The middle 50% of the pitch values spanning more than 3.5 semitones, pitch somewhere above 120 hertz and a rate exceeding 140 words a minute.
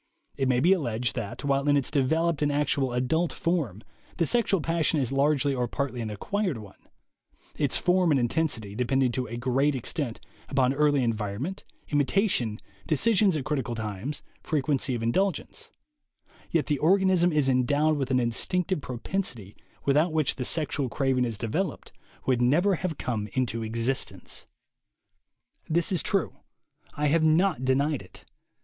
Yes: average, 4.6 semitones; medium, 140 Hz; average, 155 wpm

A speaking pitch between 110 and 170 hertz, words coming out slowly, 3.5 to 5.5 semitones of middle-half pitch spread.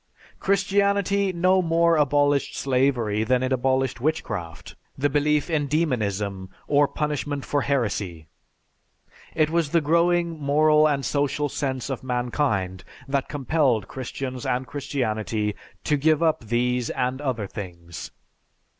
Yes: medium, 140 Hz; slow, 125 wpm; average, 4.2 semitones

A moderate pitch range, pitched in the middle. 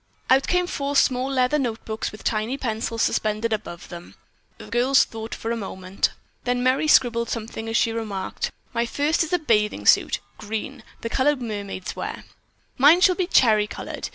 No: average, 3.8 semitones; high, 235 Hz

